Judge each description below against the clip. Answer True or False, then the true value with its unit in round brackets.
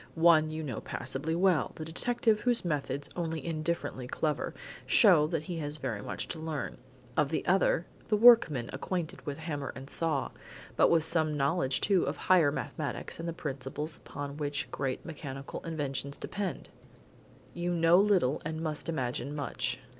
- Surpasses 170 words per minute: False (160 wpm)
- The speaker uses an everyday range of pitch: True (3.1 semitones)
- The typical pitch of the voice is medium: True (155 Hz)